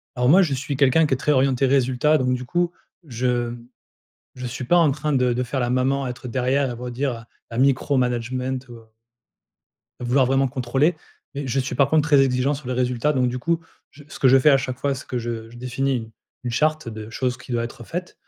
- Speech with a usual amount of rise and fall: No, narrow, 2.3 semitones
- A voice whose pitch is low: Yes, low, 130 Hz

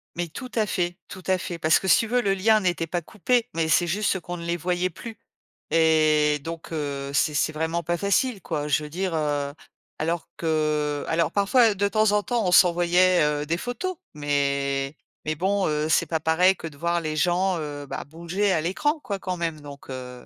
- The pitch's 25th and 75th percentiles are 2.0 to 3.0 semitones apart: No, average, 3.8 semitones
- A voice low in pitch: No, medium, 170 Hz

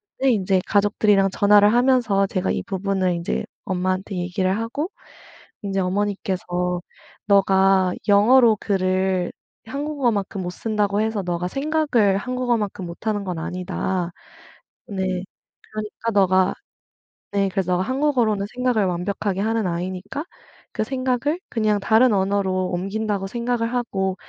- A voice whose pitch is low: No, high, 200 Hz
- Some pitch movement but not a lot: Yes, average, 3.3 semitones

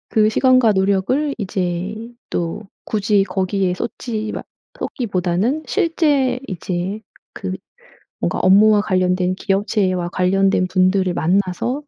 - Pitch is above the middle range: Yes, high, 195 Hz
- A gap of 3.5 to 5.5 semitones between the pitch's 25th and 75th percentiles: No, average, 3.1 semitones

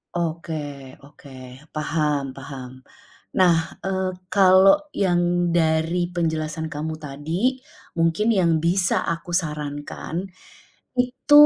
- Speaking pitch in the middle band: Yes, medium, 165 Hz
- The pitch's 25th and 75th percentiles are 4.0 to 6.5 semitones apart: No, average, 2.8 semitones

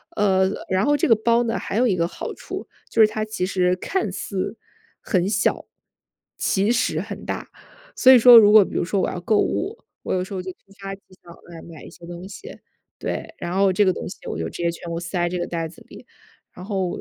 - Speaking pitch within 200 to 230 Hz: No, high, 190 Hz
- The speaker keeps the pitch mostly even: No, average, 3.6 semitones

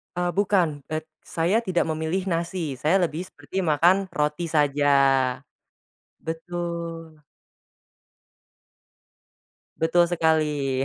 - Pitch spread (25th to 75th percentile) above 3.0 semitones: No, narrow, 2.4 semitones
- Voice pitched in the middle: Yes, medium, 165 Hz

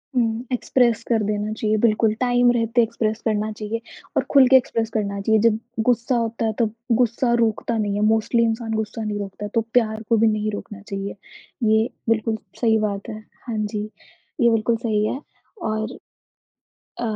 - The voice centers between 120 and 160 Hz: No, high, 220 Hz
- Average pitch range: No, narrow, 1.5 semitones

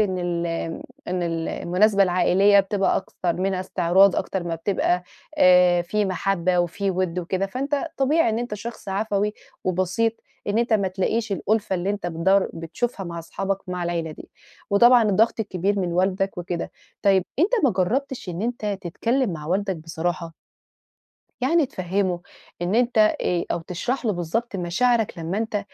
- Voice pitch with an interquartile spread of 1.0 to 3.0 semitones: No, average, 3.4 semitones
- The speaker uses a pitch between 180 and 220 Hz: Yes, high, 190 Hz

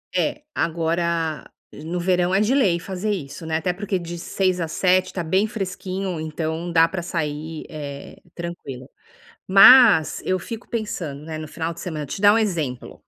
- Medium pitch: Yes, medium, 170 Hz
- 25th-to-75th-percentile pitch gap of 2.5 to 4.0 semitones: Yes, average, 3.1 semitones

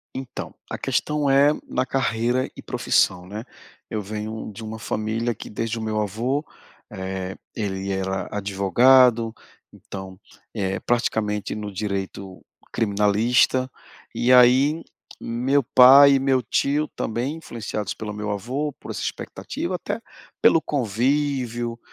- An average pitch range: Yes, average, 3.9 semitones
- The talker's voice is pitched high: No, low, 115 Hz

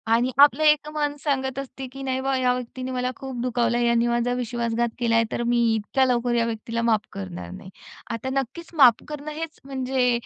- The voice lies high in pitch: Yes, very high, 250 Hz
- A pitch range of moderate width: No, narrow, 2.3 semitones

